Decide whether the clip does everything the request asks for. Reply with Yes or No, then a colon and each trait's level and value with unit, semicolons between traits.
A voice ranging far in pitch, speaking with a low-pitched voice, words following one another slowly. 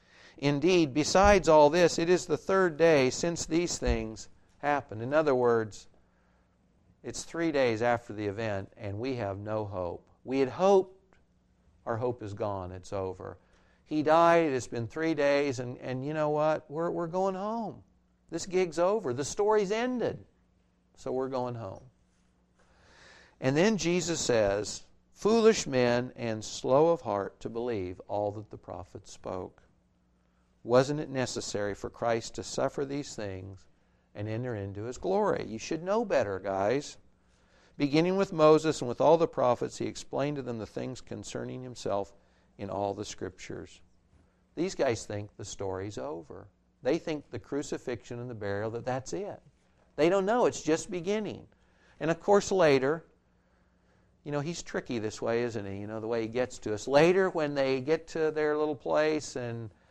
No: wide, 7.5 semitones; low, 125 Hz; average, 170 wpm